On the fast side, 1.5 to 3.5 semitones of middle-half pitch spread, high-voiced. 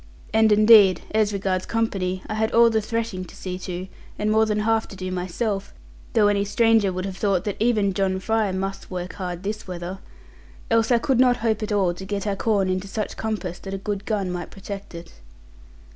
Yes: fast, 210 wpm; average, 2.7 semitones; high, 200 Hz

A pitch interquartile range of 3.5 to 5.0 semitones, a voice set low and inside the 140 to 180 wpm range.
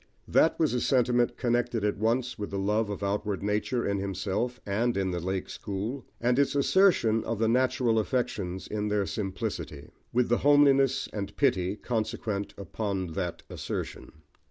Yes: average, 3.8 semitones; low, 110 Hz; average, 160 wpm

